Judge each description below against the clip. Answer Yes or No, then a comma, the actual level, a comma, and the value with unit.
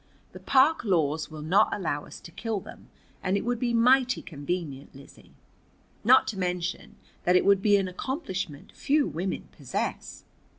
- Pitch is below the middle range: No, high, 190 Hz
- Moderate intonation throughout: No, wide, 6.2 semitones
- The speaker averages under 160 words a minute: No, average, 165 wpm